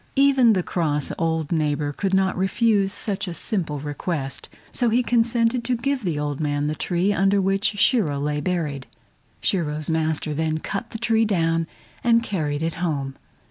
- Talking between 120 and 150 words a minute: No, average, 170 wpm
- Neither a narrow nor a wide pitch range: No, wide, 6.3 semitones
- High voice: No, medium, 175 Hz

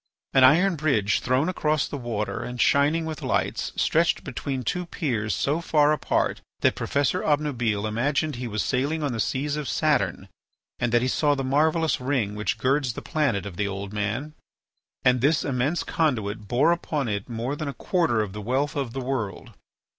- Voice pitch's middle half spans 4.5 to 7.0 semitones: Yes, average, 4.9 semitones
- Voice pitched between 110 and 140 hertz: Yes, low, 135 Hz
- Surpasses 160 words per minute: Yes, average, 185 wpm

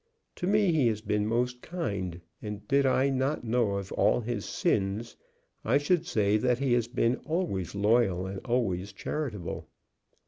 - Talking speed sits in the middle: Yes, average, 165 wpm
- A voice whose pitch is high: No, low, 115 Hz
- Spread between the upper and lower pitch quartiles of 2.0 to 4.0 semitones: No, average, 4.7 semitones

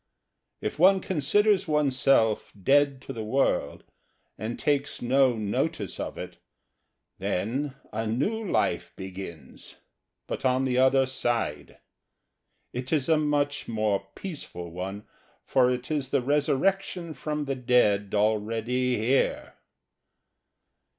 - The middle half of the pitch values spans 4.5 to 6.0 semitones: Yes, average, 5.0 semitones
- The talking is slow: Yes, slow, 115 wpm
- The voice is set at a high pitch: No, low, 130 Hz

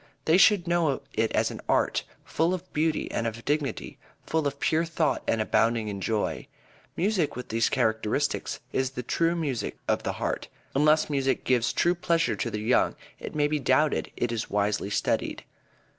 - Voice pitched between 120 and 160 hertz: Yes, medium, 140 Hz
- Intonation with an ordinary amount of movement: No, wide, 6.0 semitones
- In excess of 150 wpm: Yes, average, 185 wpm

